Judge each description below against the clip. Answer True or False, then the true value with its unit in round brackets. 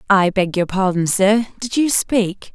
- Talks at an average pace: True (190 wpm)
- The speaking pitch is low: False (200 Hz)